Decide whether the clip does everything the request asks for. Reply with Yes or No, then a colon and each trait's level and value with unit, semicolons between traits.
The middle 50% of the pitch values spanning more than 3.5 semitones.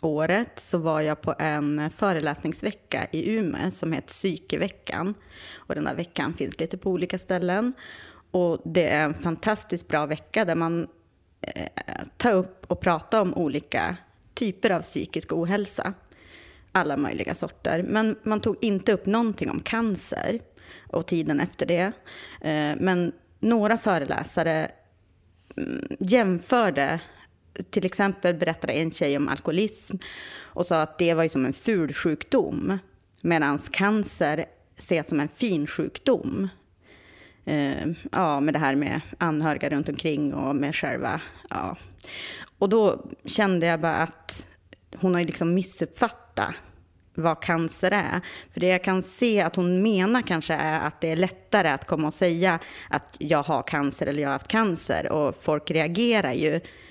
Yes: average, 4.4 semitones